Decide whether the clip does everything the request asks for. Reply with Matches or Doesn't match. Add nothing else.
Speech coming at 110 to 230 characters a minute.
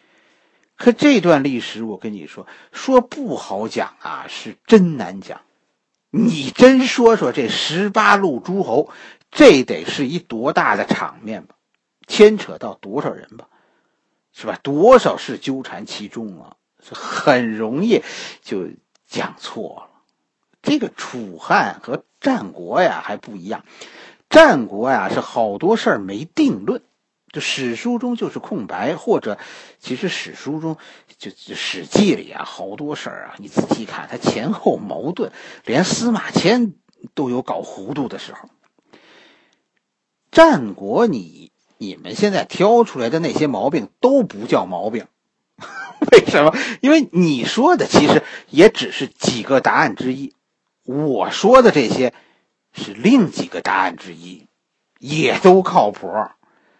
Matches